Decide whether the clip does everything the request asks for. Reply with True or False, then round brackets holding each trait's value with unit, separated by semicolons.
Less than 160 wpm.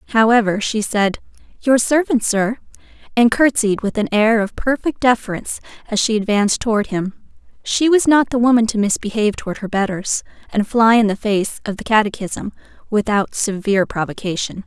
False (165 wpm)